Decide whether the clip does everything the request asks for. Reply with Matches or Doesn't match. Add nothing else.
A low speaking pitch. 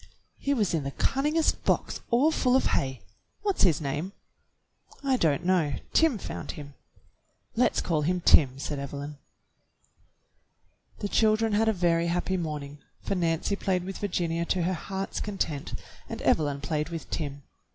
Doesn't match